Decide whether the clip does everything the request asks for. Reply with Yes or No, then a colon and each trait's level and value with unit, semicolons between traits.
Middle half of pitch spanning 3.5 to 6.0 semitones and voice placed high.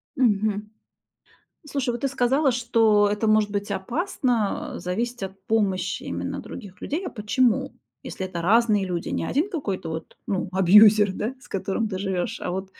Yes: average, 4.0 semitones; high, 210 Hz